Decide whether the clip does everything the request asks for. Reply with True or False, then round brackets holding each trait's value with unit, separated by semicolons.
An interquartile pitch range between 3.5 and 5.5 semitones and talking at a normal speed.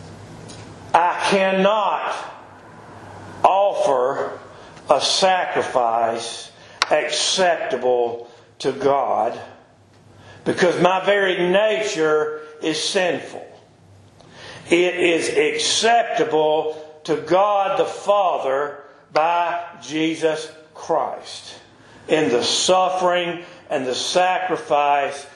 False (4.7 semitones; 70 wpm)